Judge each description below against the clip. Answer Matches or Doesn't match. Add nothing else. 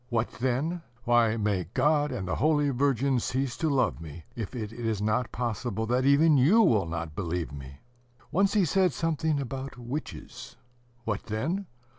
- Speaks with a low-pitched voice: Matches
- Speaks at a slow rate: Doesn't match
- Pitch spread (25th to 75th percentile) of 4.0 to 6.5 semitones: Matches